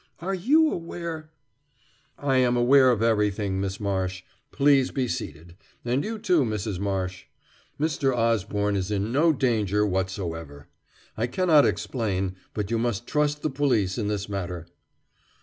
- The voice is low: Yes, low, 115 Hz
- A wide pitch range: Yes, wide, 6.3 semitones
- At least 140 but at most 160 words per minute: Yes, average, 150 wpm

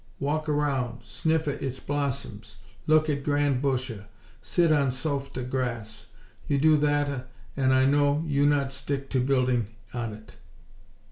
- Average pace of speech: Yes, average, 145 wpm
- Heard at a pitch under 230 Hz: Yes, medium, 140 Hz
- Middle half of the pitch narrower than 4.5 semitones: Yes, narrow, 2.5 semitones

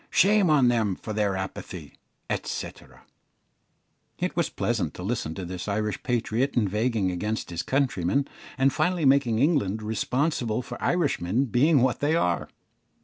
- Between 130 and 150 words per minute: Yes, average, 145 wpm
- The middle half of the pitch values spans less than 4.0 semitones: No, wide, 5.6 semitones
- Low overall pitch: Yes, low, 115 Hz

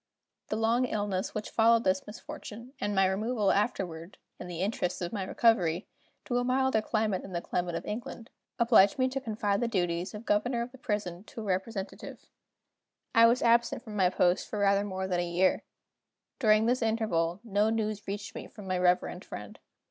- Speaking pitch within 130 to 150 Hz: No, high, 210 Hz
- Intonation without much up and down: No, average, 3.6 semitones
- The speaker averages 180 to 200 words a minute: Yes, average, 190 wpm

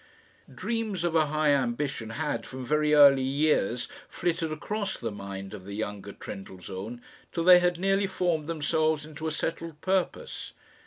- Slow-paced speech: No, average, 155 wpm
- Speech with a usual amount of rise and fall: No, wide, 6.2 semitones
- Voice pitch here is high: No, medium, 150 Hz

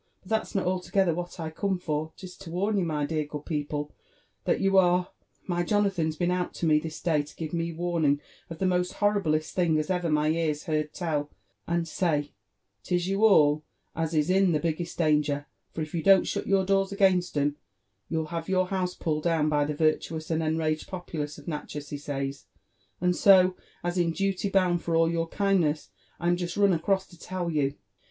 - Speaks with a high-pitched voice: No, medium, 165 Hz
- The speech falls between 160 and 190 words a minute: No, fast, 205 wpm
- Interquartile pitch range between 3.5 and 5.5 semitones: No, average, 3.1 semitones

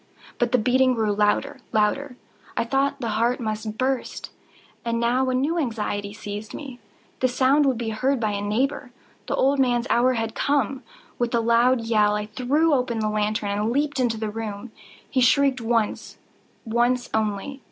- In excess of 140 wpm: Yes, average, 170 wpm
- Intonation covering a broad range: No, average, 3.2 semitones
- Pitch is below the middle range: No, high, 235 Hz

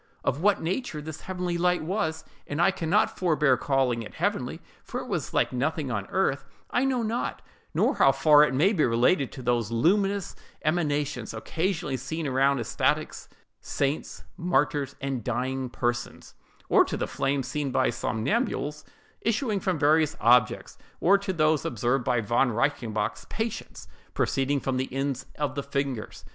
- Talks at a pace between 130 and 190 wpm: Yes, average, 160 wpm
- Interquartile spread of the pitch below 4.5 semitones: No, average, 5.2 semitones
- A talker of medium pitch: Yes, medium, 145 Hz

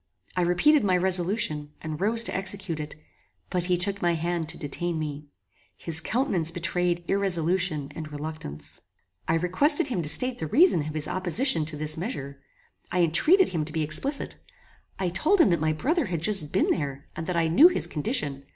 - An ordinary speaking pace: Yes, average, 190 wpm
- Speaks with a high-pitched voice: No, medium, 175 Hz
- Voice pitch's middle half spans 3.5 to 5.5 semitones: Yes, average, 3.9 semitones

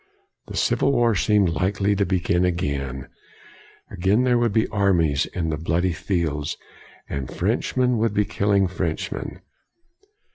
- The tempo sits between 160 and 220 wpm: No, slow, 135 wpm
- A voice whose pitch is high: No, very low, 95 Hz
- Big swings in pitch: No, average, 4.1 semitones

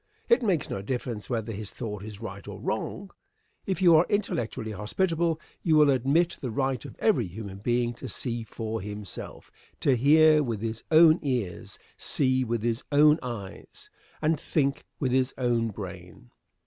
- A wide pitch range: Yes, wide, 5.8 semitones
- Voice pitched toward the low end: Yes, low, 125 Hz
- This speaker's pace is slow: No, average, 165 wpm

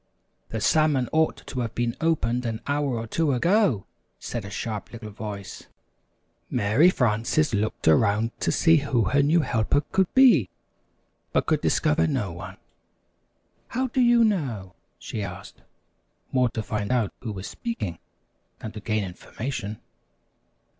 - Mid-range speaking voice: No, low, 115 Hz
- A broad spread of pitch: Yes, wide, 6.3 semitones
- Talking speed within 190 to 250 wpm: No, average, 145 wpm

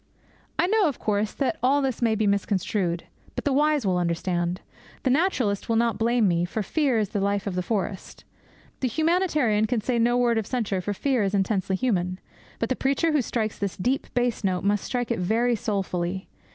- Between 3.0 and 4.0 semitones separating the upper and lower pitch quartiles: No, average, 4.7 semitones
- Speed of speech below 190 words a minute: No, fast, 205 wpm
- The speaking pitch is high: Yes, high, 220 Hz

